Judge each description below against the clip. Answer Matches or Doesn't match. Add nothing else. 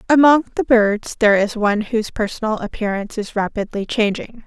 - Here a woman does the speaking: Matches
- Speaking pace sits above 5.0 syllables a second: Matches